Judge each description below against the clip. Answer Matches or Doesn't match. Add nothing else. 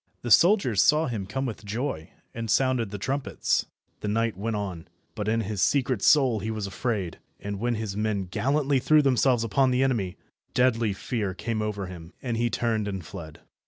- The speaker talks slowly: Doesn't match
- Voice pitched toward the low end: Matches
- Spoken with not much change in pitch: Doesn't match